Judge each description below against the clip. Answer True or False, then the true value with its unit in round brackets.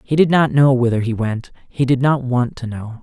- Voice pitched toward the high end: False (130 Hz)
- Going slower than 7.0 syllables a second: True (5.0 syllables/s)